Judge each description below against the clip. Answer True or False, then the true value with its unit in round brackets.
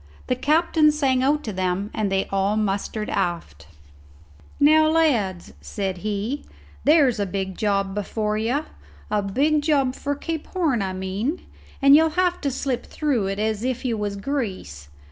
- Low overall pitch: False (220 Hz)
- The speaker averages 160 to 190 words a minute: True (165 wpm)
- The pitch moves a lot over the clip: True (6.6 semitones)